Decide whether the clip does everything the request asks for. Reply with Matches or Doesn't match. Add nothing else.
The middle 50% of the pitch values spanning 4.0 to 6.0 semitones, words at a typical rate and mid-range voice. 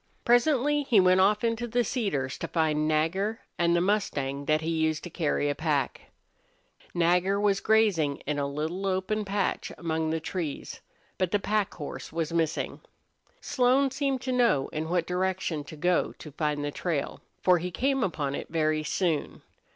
Matches